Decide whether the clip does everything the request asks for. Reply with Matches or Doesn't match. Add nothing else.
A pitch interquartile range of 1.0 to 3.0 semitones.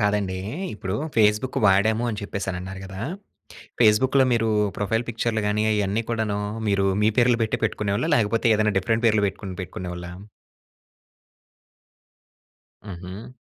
Matches